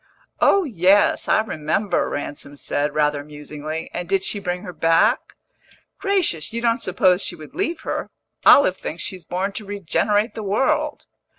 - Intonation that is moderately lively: No, wide, 5.8 semitones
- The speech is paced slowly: No, average, 160 wpm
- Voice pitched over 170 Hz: Yes, medium, 185 Hz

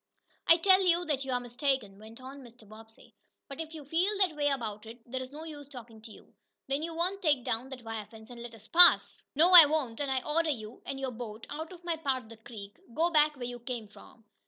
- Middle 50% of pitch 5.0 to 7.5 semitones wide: Yes, wide, 5.5 semitones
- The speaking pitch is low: No, very high, 265 Hz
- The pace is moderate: No, fast, 255 wpm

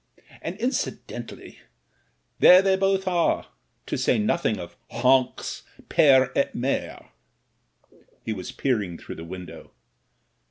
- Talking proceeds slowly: Yes, slow, 115 wpm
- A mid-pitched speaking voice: No, low, 130 Hz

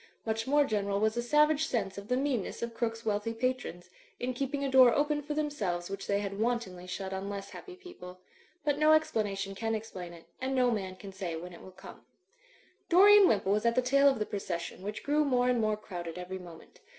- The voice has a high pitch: Yes, high, 220 Hz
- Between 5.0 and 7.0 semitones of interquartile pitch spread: Yes, wide, 5.6 semitones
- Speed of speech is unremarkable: No, fast, 220 wpm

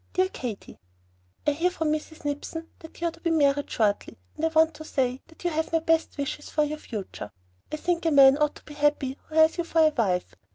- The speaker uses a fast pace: Yes, fast, 240 wpm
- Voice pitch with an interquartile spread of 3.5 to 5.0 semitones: No, narrow, 2.5 semitones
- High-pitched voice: Yes, very high, 305 Hz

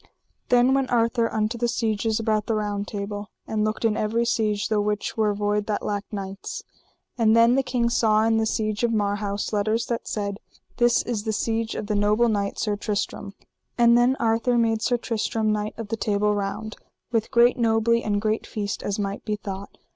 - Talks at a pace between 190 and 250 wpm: Yes, average, 200 wpm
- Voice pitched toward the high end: Yes, high, 215 Hz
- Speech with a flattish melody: Yes, narrow, 1.9 semitones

